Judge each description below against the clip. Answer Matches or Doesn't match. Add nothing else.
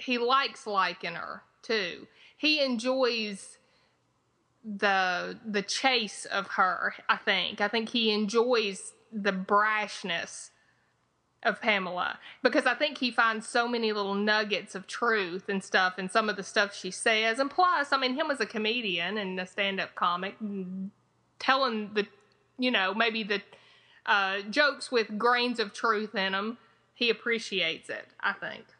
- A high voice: Matches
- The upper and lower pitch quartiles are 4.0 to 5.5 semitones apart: Doesn't match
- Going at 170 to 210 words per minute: Doesn't match